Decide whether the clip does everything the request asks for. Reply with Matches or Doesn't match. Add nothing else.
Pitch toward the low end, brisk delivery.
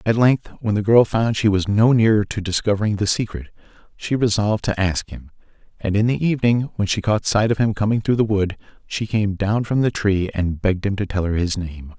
Matches